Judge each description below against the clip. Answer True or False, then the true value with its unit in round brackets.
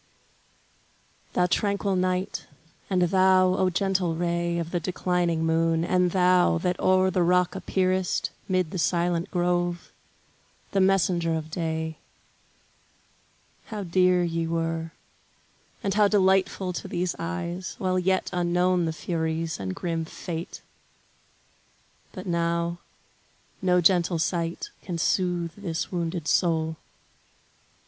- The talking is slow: True (120 wpm)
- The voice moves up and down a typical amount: False (1.8 semitones)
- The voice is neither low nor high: True (175 Hz)